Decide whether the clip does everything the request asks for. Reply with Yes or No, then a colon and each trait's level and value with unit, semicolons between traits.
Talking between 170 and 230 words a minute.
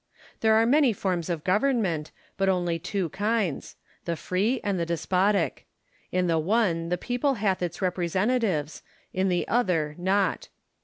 No: average, 150 wpm